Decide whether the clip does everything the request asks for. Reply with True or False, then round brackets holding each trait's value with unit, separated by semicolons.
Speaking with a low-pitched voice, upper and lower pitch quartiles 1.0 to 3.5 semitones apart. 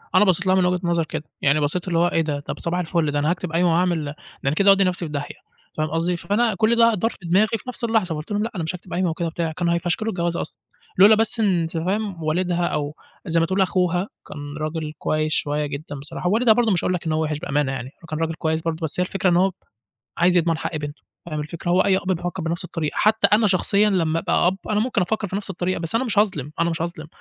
False (175 Hz; 3.2 semitones)